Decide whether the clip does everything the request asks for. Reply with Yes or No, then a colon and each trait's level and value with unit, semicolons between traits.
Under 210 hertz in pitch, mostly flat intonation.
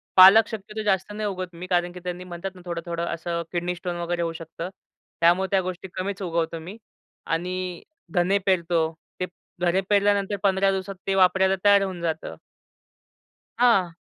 Yes: medium, 185 Hz; narrow, 2.0 semitones